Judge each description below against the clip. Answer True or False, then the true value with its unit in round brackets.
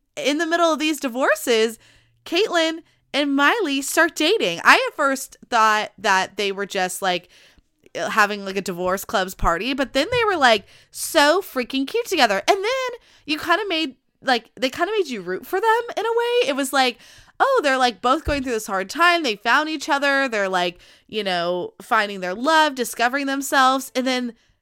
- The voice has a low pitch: False (270 Hz)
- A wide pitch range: True (7.0 semitones)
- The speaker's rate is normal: True (195 wpm)